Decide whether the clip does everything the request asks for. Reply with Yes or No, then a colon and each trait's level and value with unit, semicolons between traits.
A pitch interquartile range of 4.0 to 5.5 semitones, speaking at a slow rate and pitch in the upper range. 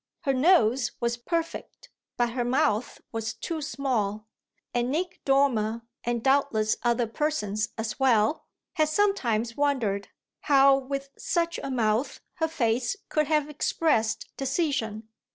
Yes: average, 4.9 semitones; slow, 130 wpm; very high, 255 Hz